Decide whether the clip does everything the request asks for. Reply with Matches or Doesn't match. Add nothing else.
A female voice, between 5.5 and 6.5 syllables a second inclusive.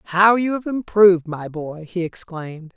Doesn't match